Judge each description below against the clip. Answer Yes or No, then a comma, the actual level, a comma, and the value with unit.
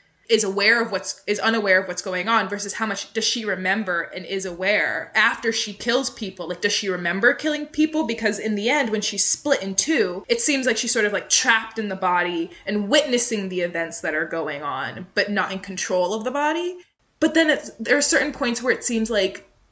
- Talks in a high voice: Yes, high, 210 Hz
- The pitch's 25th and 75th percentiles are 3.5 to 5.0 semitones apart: Yes, average, 4.1 semitones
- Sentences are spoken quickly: Yes, fast, 230 wpm